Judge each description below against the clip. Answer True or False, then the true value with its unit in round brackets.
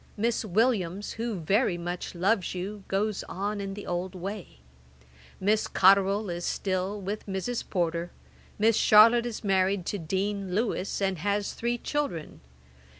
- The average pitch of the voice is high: True (195 Hz)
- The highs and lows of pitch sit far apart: False (2.6 semitones)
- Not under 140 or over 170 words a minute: True (145 wpm)